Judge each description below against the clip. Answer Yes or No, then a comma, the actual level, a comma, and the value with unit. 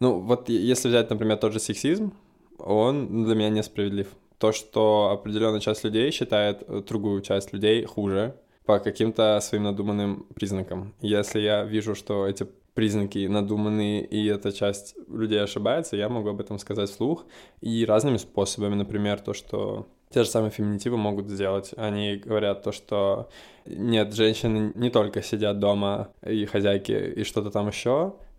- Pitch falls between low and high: No, low, 105 Hz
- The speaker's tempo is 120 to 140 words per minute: No, average, 155 wpm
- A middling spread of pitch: No, narrow, 1.4 semitones